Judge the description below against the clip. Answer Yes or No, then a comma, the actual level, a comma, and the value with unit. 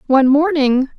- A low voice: No, very high, 285 Hz